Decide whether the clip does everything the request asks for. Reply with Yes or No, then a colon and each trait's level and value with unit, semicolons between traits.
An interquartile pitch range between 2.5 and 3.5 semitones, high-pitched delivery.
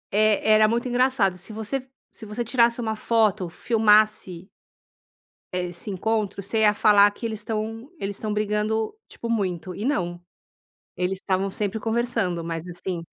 Yes: average, 2.8 semitones; high, 210 Hz